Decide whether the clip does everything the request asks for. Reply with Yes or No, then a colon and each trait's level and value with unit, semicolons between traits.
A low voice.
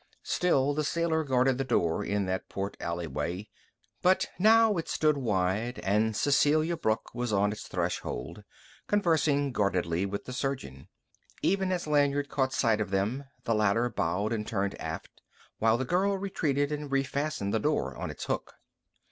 Yes: low, 125 Hz